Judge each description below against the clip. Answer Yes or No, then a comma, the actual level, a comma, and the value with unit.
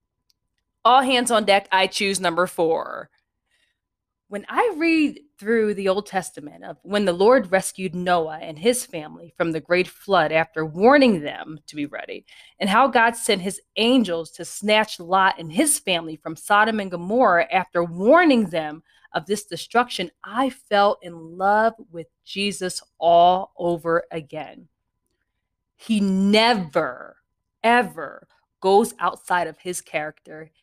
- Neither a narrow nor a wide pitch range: Yes, average, 4.8 semitones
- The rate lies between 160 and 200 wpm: No, average, 145 wpm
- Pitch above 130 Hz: Yes, high, 190 Hz